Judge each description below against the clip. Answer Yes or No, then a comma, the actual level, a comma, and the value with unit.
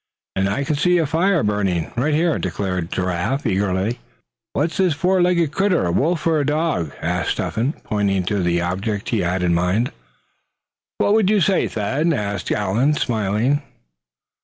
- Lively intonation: Yes, wide, 8.8 semitones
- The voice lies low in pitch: Yes, low, 115 Hz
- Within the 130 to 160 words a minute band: No, average, 170 wpm